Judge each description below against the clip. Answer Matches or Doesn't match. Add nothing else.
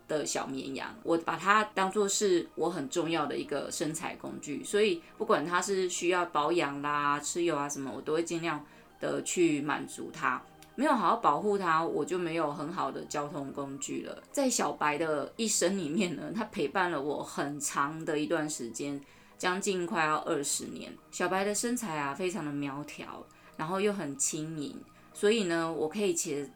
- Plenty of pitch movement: Doesn't match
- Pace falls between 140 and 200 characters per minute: Doesn't match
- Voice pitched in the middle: Matches